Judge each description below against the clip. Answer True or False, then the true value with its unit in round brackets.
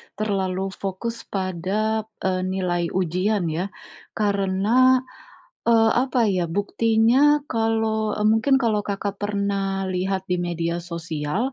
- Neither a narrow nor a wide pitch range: True (3.1 semitones)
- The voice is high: True (200 Hz)